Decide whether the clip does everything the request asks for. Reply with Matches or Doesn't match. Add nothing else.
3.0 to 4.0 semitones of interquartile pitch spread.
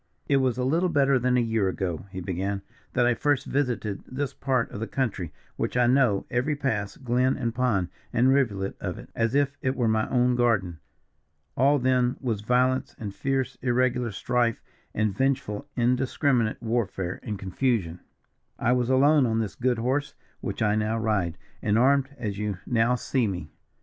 Matches